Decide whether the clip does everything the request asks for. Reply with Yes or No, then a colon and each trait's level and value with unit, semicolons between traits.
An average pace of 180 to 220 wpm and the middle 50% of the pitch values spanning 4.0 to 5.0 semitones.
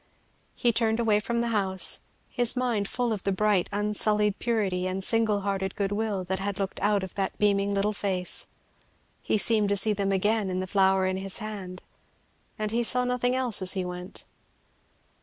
No: average, 195 wpm; narrow, 2.5 semitones